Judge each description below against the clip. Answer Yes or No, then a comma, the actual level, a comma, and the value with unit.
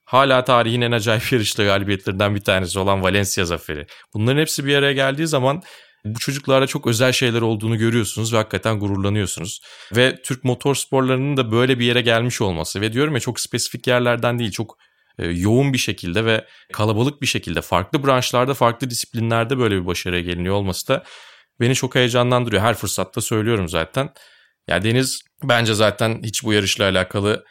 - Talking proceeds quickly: Yes, fast, 170 wpm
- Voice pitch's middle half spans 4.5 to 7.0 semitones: No, average, 4.0 semitones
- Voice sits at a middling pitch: No, low, 115 Hz